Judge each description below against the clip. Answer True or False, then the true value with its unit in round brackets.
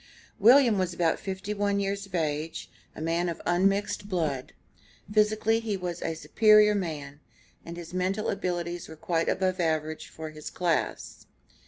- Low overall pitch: False (180 Hz)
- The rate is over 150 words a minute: True (160 wpm)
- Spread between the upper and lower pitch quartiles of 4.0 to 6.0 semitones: False (3.6 semitones)